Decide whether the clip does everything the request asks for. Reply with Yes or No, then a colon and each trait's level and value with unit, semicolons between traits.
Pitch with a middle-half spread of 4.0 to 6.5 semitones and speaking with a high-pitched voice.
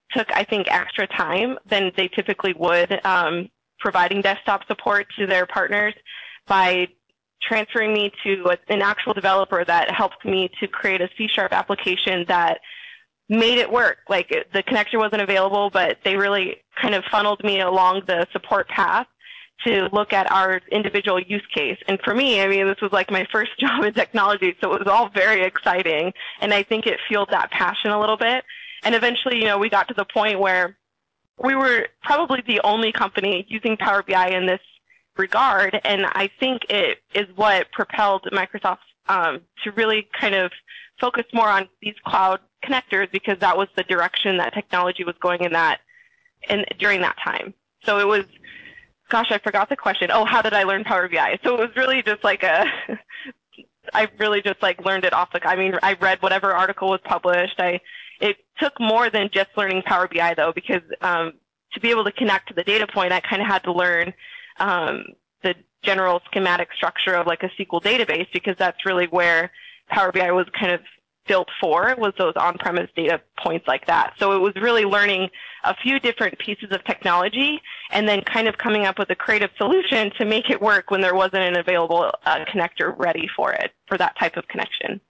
No: average, 3.0 semitones; high, 200 Hz